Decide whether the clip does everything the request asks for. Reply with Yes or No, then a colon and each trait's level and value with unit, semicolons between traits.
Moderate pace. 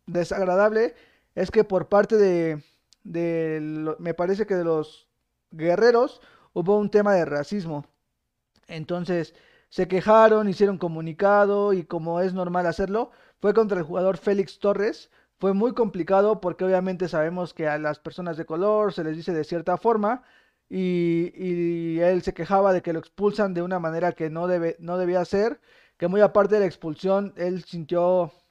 Yes: average, 165 wpm